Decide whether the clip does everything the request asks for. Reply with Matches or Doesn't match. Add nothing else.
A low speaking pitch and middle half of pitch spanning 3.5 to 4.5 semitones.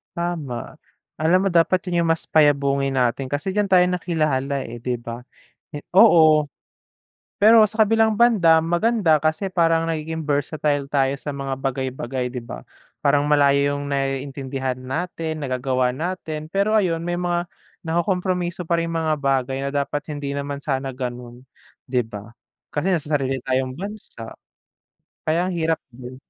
Doesn't match